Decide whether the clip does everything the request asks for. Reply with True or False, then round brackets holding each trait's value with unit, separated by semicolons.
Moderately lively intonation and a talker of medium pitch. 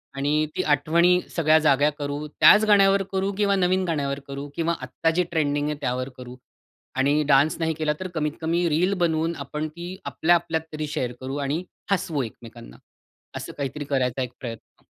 True (3.5 semitones; 150 Hz)